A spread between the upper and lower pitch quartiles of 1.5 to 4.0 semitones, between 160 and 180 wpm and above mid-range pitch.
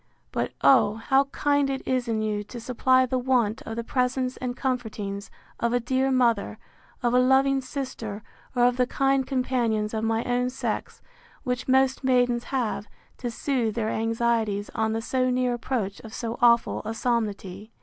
Yes: narrow, 2.6 semitones; average, 175 wpm; high, 245 Hz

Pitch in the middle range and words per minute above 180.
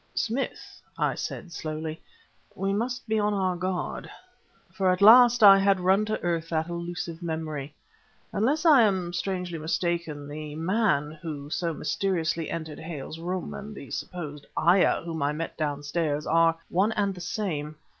No: medium, 175 Hz; average, 155 wpm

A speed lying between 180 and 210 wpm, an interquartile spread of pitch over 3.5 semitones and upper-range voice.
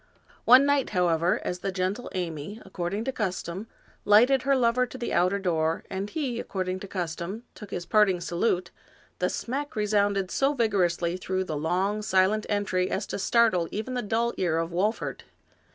No: average, 170 wpm; average, 4.2 semitones; high, 195 Hz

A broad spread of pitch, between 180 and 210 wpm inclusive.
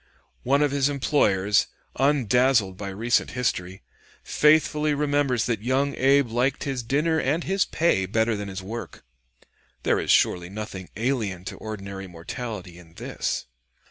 No: wide, 6.2 semitones; average, 140 wpm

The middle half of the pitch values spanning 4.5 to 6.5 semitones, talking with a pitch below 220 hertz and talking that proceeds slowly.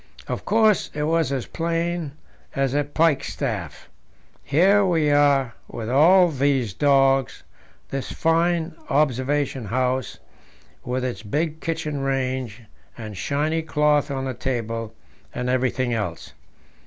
No: average, 3.8 semitones; medium, 140 Hz; slow, 120 wpm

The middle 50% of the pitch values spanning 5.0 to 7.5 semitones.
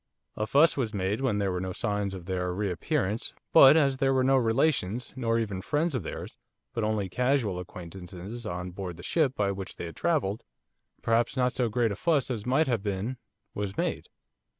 Yes: wide, 5.4 semitones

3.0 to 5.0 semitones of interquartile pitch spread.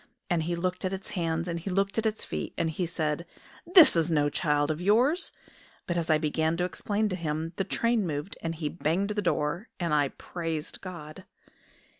Yes: average, 3.5 semitones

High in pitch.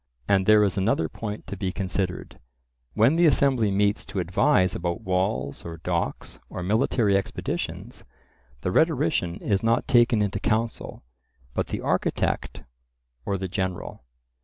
No: very low, 95 Hz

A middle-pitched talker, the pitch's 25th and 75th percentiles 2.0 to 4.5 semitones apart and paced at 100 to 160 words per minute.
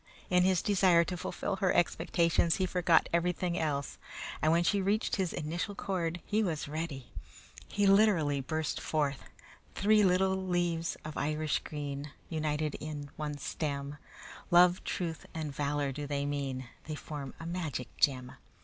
Yes: medium, 160 Hz; average, 3.6 semitones; average, 150 wpm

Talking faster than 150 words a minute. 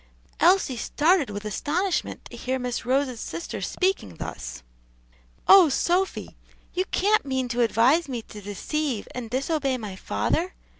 No: average, 140 wpm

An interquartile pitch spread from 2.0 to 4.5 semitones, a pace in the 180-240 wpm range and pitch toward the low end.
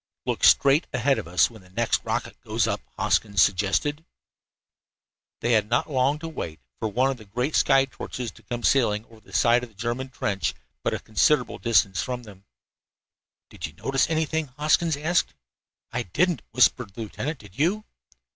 No: average, 5.3 semitones; average, 185 wpm; low, 120 Hz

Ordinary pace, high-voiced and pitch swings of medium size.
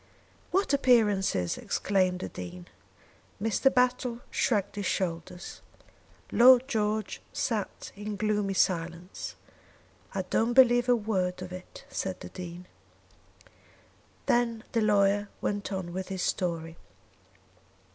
No: slow, 115 wpm; high, 200 Hz; average, 4.1 semitones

